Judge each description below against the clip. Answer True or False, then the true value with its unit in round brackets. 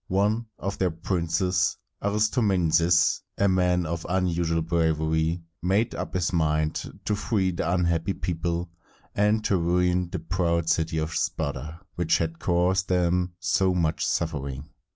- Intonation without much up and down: True (2.2 semitones)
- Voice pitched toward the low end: True (85 Hz)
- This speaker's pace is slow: False (150 wpm)